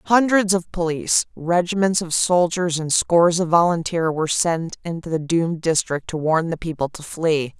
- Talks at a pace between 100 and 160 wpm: No, average, 175 wpm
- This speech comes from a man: No, female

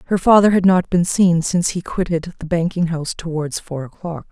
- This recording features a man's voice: No, female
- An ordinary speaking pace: No, fast, 210 wpm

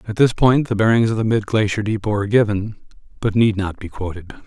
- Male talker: Yes, male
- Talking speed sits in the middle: No, fast, 230 wpm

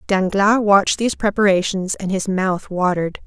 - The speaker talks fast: No, average, 145 wpm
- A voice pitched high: Yes, high, 195 Hz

